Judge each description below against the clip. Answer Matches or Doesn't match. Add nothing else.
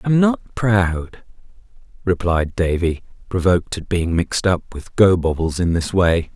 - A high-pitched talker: Doesn't match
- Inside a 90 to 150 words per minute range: Matches